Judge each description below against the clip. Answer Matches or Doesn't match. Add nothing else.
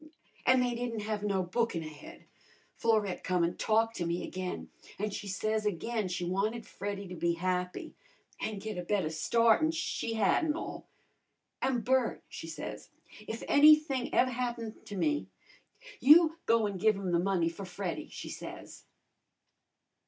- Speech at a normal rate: Matches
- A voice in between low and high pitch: Doesn't match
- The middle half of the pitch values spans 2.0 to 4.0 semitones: Doesn't match